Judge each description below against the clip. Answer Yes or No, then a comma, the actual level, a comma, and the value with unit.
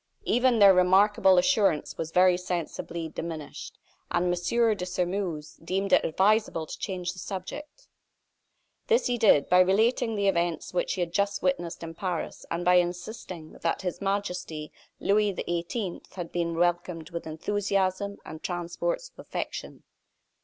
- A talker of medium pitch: Yes, medium, 180 Hz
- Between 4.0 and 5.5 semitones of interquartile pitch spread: No, average, 2.9 semitones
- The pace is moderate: Yes, average, 145 wpm